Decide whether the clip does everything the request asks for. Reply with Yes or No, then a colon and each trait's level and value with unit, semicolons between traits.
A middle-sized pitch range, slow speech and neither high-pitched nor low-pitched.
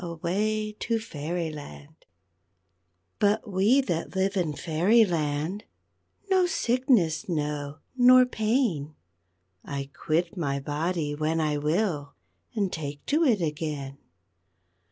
No: wide, 6.3 semitones; slow, 105 wpm; medium, 170 Hz